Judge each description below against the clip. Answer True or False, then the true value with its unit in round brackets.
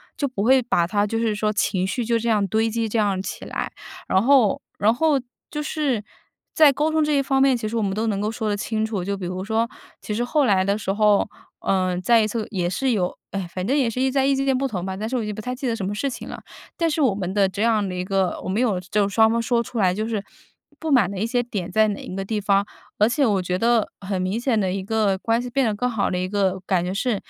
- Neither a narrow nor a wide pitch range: True (3.8 semitones)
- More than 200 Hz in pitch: True (215 Hz)